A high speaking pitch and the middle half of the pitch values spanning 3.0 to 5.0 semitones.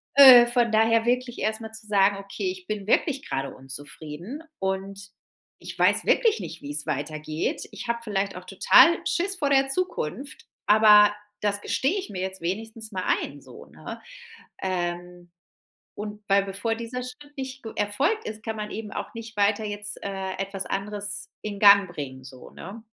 Yes: high, 210 Hz; average, 3.7 semitones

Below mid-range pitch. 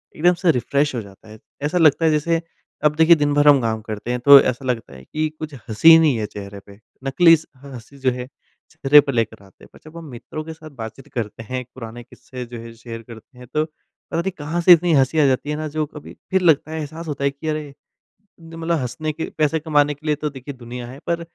No: medium, 145 Hz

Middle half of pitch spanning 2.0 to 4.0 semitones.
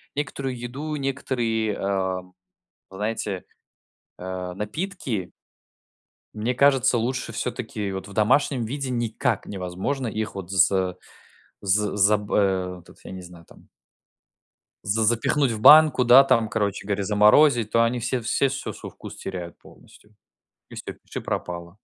No: average, 4.6 semitones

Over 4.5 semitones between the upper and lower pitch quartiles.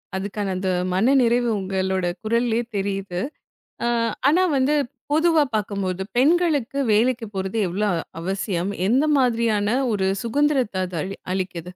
Yes: average, 4.9 semitones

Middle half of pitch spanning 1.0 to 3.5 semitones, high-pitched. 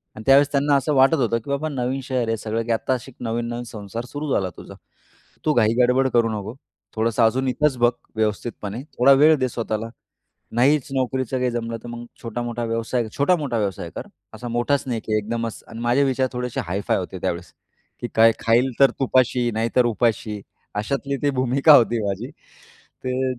No: average, 2.8 semitones; low, 120 Hz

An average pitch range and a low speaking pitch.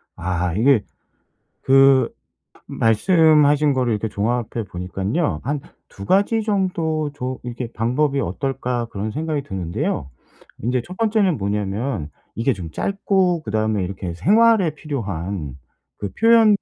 No: wide, 7.7 semitones; low, 125 Hz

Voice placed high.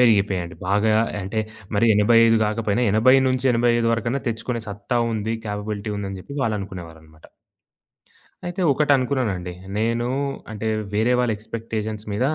No: low, 110 Hz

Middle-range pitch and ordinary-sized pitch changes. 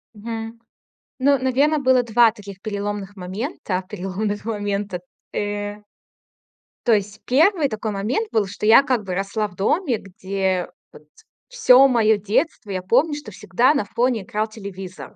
No: high, 215 Hz; average, 3.9 semitones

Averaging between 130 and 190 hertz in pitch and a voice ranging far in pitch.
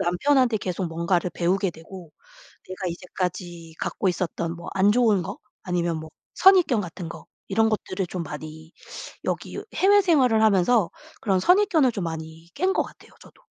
No: medium, 185 Hz; average, 4.6 semitones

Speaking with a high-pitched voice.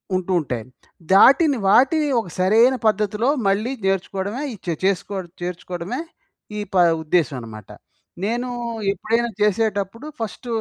Yes: high, 200 Hz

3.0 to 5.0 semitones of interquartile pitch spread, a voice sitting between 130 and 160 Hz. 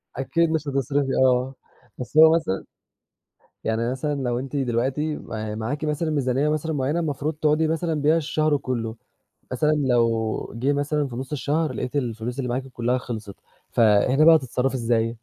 Yes: average, 3.8 semitones; low, 135 Hz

